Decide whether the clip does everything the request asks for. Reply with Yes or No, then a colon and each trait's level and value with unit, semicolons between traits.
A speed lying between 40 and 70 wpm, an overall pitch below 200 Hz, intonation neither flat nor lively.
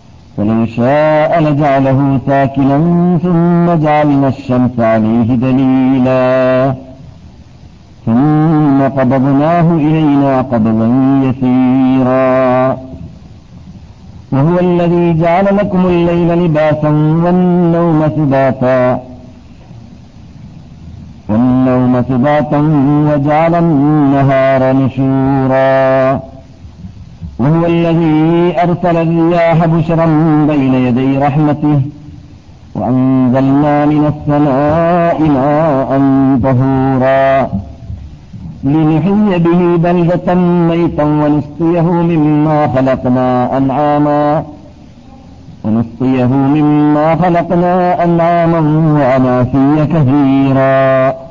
Yes: average, 65 wpm; medium, 140 Hz; average, 3.6 semitones